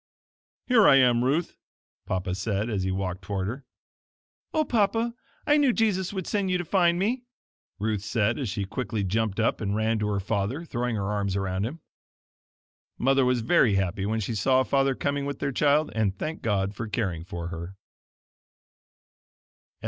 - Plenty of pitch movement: Yes, wide, 6.5 semitones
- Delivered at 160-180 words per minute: Yes, average, 175 wpm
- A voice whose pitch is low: Yes, low, 115 Hz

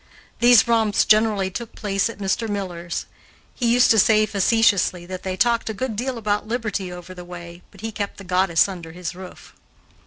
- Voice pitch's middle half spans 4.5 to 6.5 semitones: No, average, 3.5 semitones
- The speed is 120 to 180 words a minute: No, average, 190 wpm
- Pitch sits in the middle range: No, high, 200 Hz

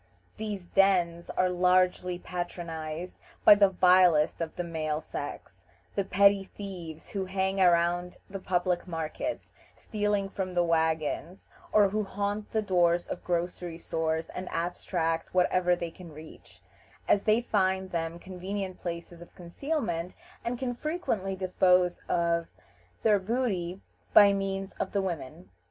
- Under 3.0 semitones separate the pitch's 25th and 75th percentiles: Yes, narrow, 2.4 semitones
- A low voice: No, medium, 180 Hz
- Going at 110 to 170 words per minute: Yes, average, 140 wpm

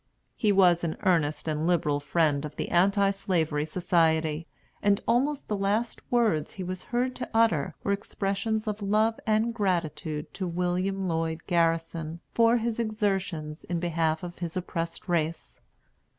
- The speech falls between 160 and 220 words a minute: No, average, 150 wpm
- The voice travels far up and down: No, average, 4.2 semitones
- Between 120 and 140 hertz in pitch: No, medium, 180 Hz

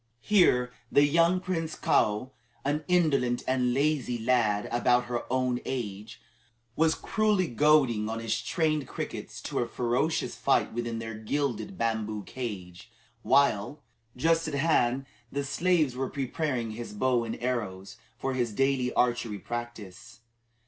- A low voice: Yes, low, 125 Hz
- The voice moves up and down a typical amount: Yes, average, 4.2 semitones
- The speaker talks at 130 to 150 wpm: Yes, average, 140 wpm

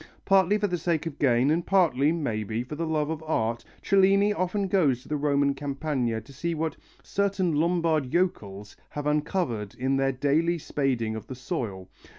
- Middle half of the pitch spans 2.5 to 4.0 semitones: No, average, 5.1 semitones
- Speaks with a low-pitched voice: No, medium, 150 Hz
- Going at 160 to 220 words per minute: Yes, average, 175 wpm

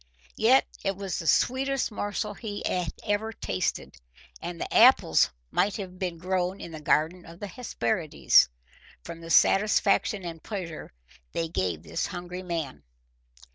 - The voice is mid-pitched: Yes, medium, 180 Hz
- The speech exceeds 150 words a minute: No, average, 145 wpm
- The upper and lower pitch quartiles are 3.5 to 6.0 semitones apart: Yes, average, 3.8 semitones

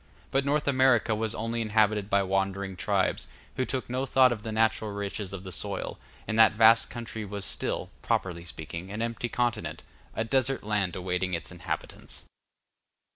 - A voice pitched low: Yes, low, 110 Hz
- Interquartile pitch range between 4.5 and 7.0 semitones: No, average, 3.2 semitones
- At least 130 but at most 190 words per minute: Yes, average, 170 wpm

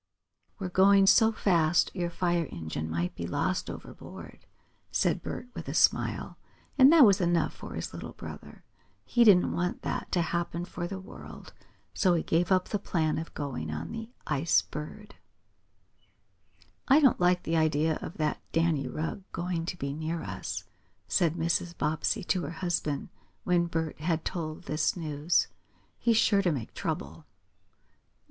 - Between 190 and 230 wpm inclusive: No, average, 160 wpm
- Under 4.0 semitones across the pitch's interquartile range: Yes, average, 3.0 semitones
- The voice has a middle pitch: Yes, medium, 170 Hz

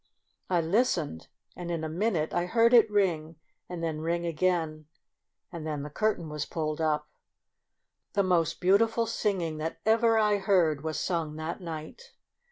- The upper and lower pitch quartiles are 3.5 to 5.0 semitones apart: Yes, average, 4.3 semitones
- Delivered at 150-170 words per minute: Yes, average, 165 wpm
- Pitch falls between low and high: Yes, medium, 170 Hz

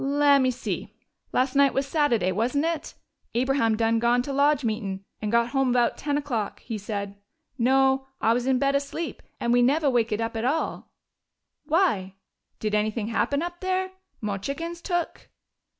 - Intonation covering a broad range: No, average, 4.1 semitones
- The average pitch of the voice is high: Yes, very high, 255 Hz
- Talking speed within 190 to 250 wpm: No, average, 165 wpm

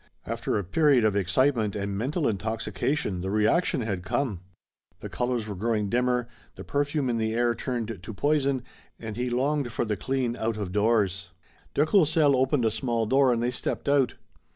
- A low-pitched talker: Yes, low, 120 Hz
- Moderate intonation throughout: Yes, average, 4.2 semitones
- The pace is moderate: Yes, average, 180 wpm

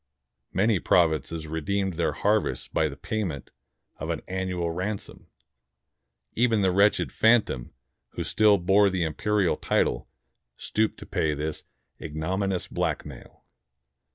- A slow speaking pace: Yes, slow, 125 wpm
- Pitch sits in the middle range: No, very low, 95 Hz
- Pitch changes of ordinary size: Yes, average, 4.3 semitones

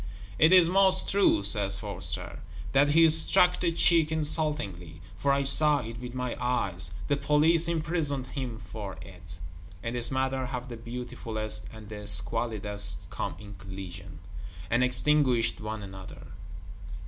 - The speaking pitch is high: No, low, 125 Hz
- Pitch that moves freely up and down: Yes, wide, 6.5 semitones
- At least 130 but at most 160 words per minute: Yes, average, 145 wpm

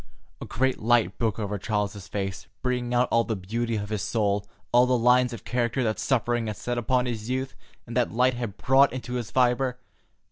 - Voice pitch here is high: No, low, 120 Hz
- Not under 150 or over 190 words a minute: No, fast, 205 wpm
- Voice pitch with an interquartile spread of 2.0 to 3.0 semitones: Yes, narrow, 2.5 semitones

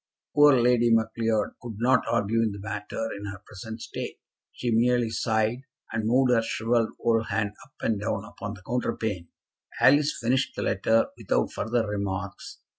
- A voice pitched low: Yes, low, 115 Hz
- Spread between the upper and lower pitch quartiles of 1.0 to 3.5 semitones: Yes, narrow, 2.5 semitones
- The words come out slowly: No, average, 160 wpm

